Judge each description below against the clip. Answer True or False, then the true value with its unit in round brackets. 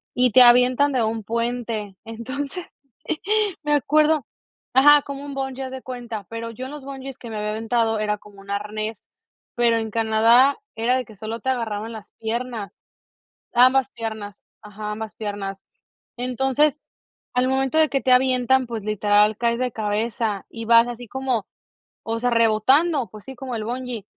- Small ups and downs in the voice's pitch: False (3.1 semitones)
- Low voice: False (235 Hz)